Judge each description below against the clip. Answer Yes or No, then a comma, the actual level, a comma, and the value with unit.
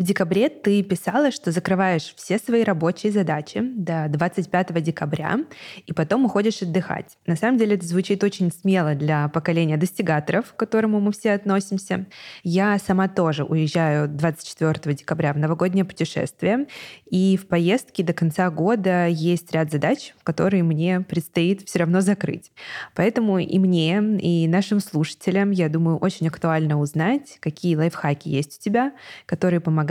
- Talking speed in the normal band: Yes, average, 150 wpm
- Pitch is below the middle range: No, medium, 180 Hz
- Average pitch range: Yes, average, 3.6 semitones